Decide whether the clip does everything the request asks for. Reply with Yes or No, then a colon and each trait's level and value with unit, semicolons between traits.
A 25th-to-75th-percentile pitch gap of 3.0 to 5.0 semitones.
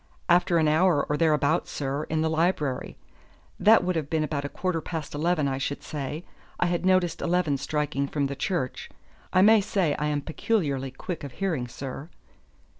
Yes: average, 3.7 semitones